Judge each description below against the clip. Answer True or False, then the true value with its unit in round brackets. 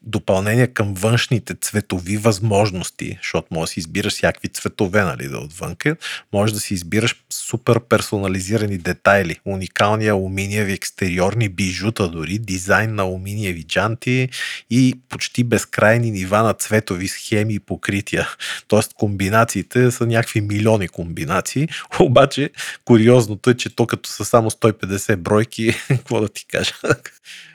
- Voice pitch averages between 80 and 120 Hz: True (110 Hz)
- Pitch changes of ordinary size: True (3.1 semitones)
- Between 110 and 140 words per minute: True (130 wpm)